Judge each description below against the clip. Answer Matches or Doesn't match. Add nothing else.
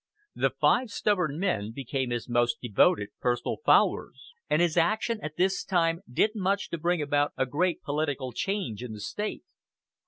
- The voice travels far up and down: Matches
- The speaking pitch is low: Doesn't match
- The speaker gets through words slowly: Doesn't match